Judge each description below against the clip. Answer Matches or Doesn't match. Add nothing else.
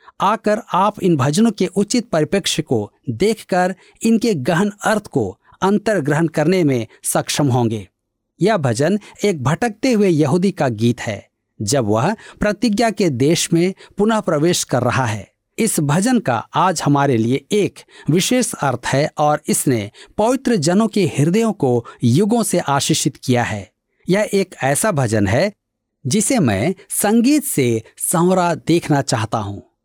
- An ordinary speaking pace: Matches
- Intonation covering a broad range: Matches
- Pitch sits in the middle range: Matches